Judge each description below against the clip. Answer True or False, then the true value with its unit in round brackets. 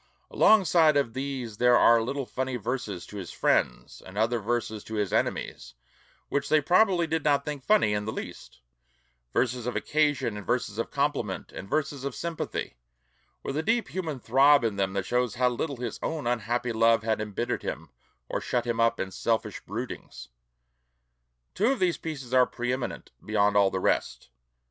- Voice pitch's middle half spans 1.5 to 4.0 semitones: False (4.8 semitones)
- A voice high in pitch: False (125 Hz)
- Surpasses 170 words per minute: True (180 wpm)